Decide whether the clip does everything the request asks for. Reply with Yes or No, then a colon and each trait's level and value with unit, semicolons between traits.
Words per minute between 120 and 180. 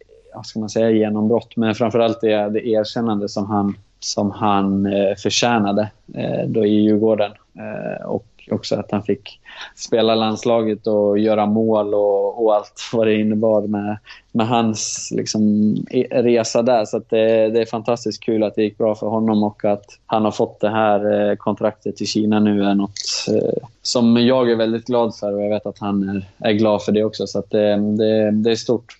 No: fast, 195 wpm